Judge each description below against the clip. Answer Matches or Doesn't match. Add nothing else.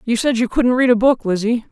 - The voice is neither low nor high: Doesn't match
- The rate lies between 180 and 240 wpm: Doesn't match